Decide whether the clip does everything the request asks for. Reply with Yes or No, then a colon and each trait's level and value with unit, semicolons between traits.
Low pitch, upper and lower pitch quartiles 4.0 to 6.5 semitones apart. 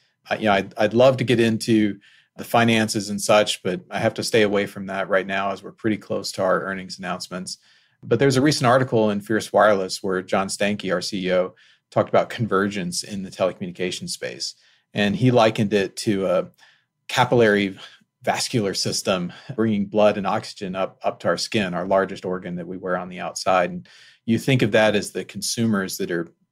No: low, 105 Hz; average, 3.4 semitones